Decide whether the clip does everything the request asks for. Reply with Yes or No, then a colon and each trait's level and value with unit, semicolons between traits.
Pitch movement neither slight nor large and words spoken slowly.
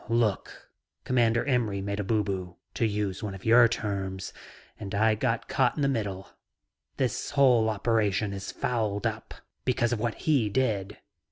No: average, 3.0 semitones; average, 160 wpm